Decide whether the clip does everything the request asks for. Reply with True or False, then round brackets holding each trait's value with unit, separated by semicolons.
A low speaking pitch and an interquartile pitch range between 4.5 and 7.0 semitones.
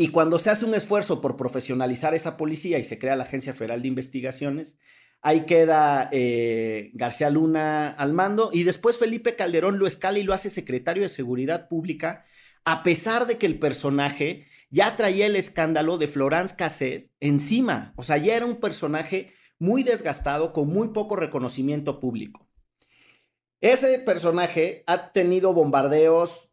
False (160 Hz; 5.3 semitones)